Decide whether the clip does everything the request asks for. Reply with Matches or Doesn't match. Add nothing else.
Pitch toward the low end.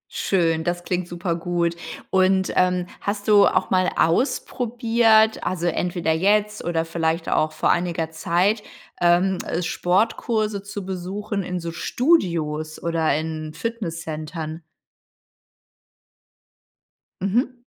Doesn't match